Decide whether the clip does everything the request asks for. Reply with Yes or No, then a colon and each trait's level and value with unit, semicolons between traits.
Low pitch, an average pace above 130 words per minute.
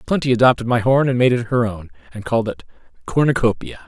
Yes: low, 120 Hz; average, 200 wpm